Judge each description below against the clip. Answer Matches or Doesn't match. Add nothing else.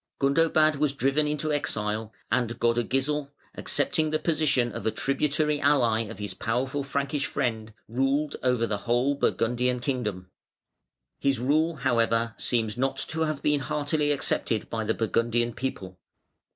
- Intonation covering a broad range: Doesn't match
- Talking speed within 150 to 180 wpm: Doesn't match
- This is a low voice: Matches